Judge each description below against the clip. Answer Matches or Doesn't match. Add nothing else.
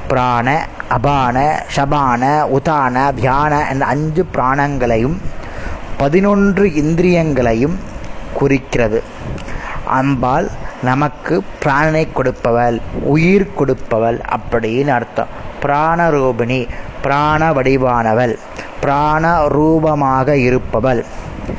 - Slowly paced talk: Matches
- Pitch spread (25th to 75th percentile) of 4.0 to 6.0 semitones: Doesn't match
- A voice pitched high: Doesn't match